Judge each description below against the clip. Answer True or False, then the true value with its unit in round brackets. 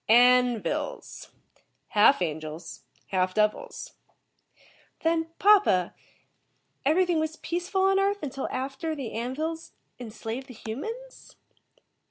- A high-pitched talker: True (270 Hz)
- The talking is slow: True (100 wpm)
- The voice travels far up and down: True (7.9 semitones)